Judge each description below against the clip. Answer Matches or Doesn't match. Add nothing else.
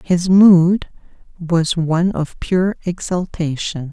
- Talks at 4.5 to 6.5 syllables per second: Doesn't match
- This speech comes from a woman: Matches